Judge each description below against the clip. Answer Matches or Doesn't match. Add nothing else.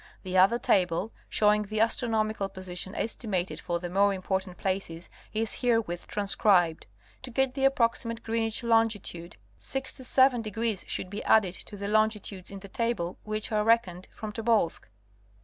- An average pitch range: Matches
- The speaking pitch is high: Matches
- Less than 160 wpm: Matches